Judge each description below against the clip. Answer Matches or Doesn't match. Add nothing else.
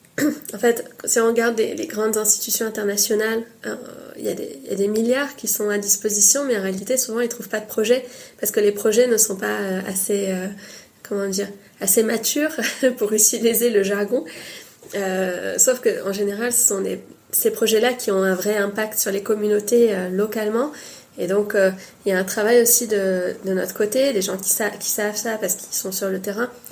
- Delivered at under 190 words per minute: Doesn't match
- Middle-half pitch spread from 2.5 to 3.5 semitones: Matches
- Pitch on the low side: Doesn't match